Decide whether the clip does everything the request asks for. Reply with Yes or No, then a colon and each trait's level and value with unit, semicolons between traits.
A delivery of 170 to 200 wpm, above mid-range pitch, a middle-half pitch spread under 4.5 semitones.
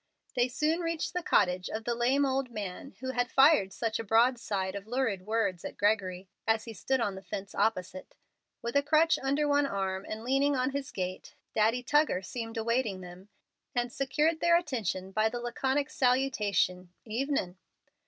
No: average, 175 wpm; high, 235 Hz; wide, 5.5 semitones